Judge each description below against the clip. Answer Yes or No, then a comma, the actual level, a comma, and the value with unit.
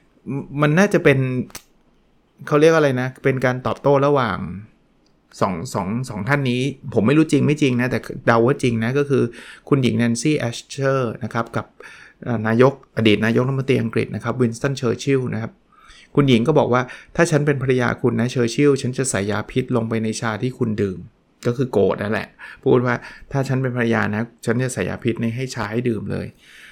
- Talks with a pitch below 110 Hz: No, low, 125 Hz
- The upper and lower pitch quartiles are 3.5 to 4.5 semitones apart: No, average, 3.1 semitones